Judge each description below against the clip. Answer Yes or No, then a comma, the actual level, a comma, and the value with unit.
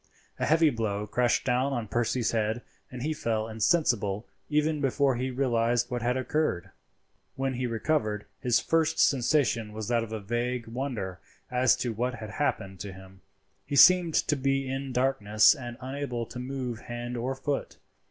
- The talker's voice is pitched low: Yes, low, 125 Hz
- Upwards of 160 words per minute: Yes, average, 170 wpm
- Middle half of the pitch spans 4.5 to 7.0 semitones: No, average, 3.4 semitones